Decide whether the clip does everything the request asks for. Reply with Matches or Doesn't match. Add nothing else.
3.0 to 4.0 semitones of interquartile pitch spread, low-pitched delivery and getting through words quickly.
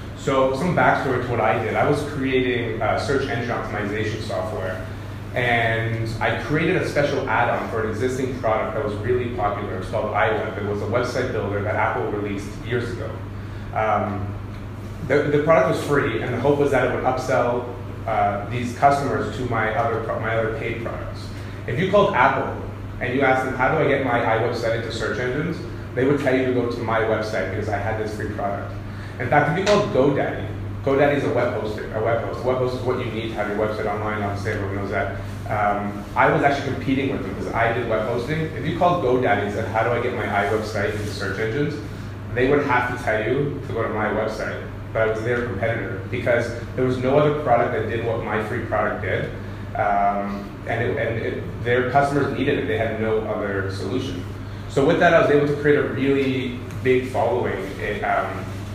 Matches